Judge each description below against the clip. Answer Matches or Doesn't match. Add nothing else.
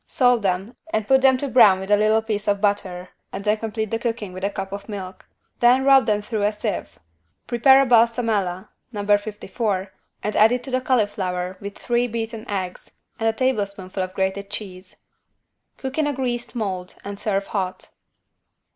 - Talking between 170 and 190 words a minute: Matches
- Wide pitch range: Doesn't match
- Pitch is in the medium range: Doesn't match